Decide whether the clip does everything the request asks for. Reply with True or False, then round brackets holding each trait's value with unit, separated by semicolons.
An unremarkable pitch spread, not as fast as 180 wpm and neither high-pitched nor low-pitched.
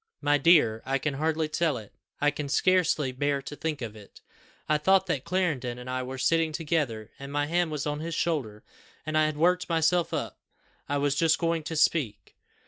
False (3.4 semitones; 205 wpm; 150 Hz)